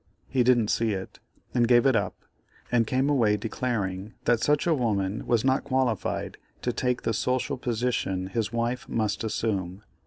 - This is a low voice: Yes, low, 115 Hz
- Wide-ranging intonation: No, average, 3.2 semitones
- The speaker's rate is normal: Yes, average, 165 wpm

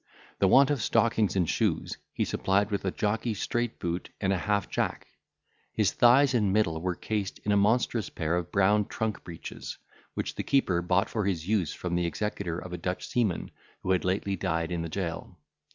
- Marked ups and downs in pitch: No, average, 3.6 semitones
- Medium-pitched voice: No, very low, 95 Hz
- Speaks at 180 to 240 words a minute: Yes, average, 200 wpm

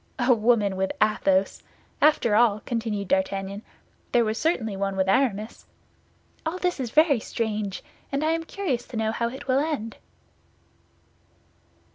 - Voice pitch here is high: Yes, high, 225 Hz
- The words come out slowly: No, average, 145 wpm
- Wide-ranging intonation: No, average, 5.0 semitones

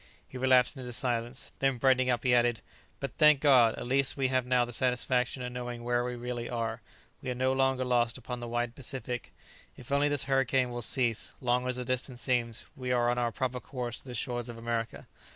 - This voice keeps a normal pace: No, fast, 220 wpm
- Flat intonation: Yes, narrow, 1.3 semitones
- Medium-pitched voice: No, low, 125 Hz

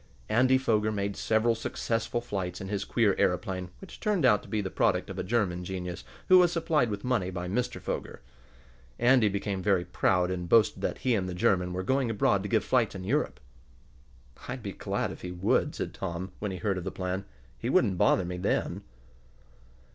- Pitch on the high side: No, low, 100 Hz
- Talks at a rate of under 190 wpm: No, average, 200 wpm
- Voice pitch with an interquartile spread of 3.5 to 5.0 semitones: Yes, average, 4.2 semitones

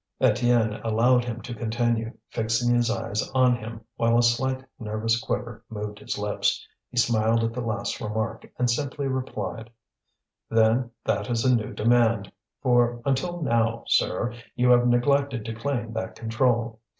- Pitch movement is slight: Yes, narrow, 1.6 semitones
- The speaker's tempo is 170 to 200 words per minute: No, average, 155 wpm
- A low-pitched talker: Yes, low, 115 Hz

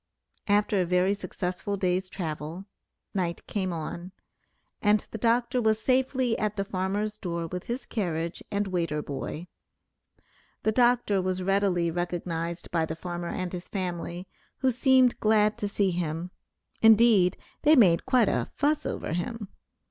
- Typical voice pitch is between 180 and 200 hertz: Yes, high, 190 Hz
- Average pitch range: Yes, average, 3.8 semitones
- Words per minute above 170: No, average, 150 wpm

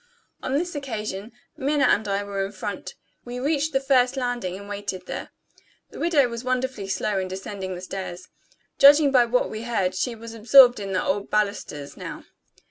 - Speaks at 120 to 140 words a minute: No, average, 185 wpm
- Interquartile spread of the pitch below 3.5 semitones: No, average, 4.9 semitones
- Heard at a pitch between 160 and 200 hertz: No, high, 220 Hz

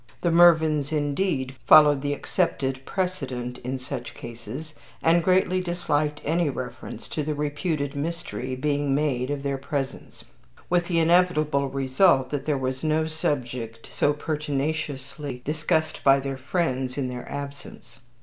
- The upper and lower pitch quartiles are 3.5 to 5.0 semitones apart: No, average, 3.1 semitones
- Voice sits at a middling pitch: Yes, medium, 145 Hz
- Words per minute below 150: Yes, average, 140 wpm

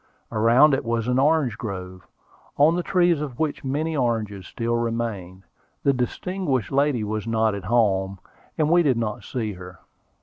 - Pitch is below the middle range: Yes, low, 115 Hz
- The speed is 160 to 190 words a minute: Yes, average, 165 wpm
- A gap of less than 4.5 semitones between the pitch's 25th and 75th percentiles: No, average, 5.2 semitones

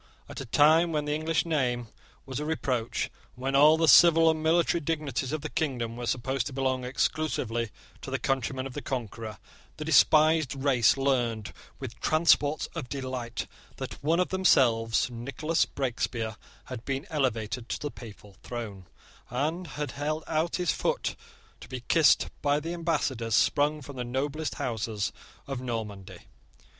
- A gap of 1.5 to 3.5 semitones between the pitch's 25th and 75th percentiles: No, average, 4.5 semitones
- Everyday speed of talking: Yes, average, 160 wpm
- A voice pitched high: No, low, 135 Hz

